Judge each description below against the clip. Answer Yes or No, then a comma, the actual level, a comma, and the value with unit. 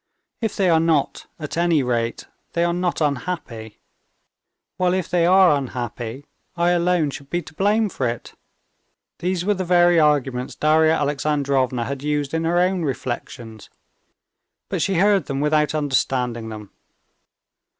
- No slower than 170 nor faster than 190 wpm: No, average, 150 wpm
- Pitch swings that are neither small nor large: Yes, average, 4.8 semitones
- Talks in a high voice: No, medium, 150 Hz